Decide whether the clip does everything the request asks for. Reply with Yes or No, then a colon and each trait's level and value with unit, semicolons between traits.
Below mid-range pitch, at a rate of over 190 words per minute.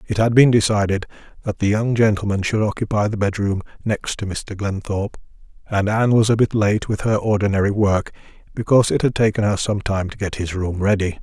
Yes: low, 105 Hz; fast, 205 wpm